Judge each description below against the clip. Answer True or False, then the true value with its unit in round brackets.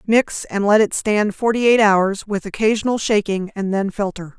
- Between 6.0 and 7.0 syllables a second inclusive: False (4.7 syllables/s)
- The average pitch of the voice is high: True (205 Hz)